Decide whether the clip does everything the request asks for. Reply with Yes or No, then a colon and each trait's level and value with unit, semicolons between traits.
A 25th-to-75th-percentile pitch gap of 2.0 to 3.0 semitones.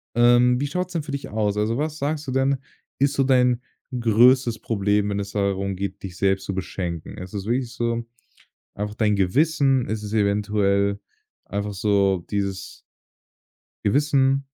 No: average, 5.0 semitones